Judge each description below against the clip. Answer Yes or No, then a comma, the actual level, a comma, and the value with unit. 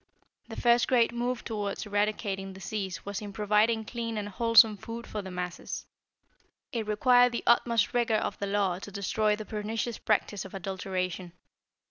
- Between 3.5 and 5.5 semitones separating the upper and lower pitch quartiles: No, average, 2.8 semitones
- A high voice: Yes, high, 210 Hz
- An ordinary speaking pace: Yes, average, 160 wpm